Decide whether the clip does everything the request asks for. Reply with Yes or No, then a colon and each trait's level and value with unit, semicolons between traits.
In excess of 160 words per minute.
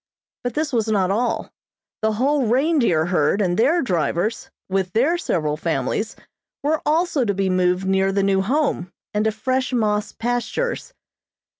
No: average, 155 wpm